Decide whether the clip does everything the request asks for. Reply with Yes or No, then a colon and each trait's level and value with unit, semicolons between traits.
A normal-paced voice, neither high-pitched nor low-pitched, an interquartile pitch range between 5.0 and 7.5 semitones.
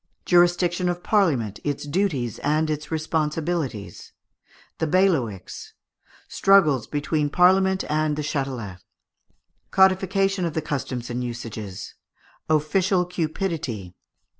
No: slow, 100 wpm; medium, 155 Hz; wide, 5.4 semitones